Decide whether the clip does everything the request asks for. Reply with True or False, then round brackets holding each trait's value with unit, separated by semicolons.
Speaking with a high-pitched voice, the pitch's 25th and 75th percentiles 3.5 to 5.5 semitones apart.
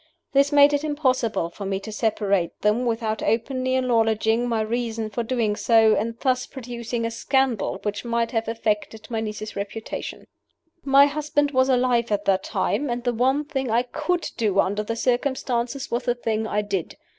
False (235 Hz; 2.9 semitones)